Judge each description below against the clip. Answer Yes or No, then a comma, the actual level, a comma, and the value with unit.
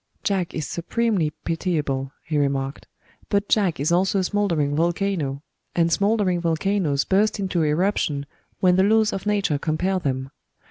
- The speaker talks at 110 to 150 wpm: Yes, average, 145 wpm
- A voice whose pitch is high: No, medium, 175 Hz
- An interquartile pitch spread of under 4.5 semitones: No, average, 4.9 semitones